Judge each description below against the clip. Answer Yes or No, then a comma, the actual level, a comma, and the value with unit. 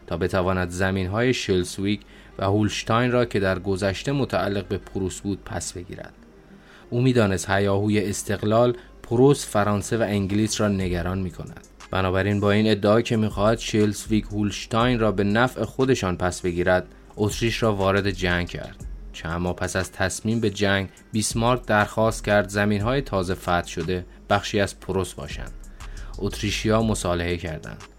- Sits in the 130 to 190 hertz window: No, low, 100 Hz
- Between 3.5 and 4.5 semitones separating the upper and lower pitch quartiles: No, average, 2.8 semitones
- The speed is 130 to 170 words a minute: Yes, average, 150 wpm